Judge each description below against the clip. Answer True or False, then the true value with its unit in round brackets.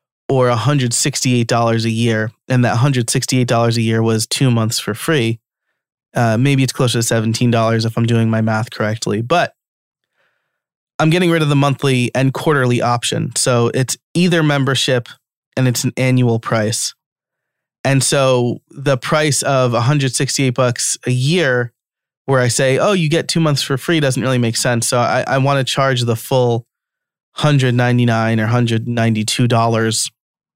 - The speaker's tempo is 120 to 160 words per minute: False (185 wpm)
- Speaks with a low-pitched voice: True (125 Hz)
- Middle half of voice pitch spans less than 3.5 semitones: True (2.7 semitones)